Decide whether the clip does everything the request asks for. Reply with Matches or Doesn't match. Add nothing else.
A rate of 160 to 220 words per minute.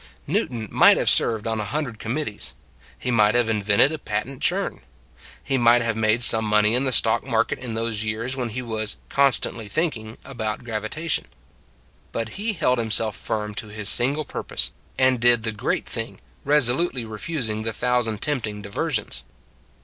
Matches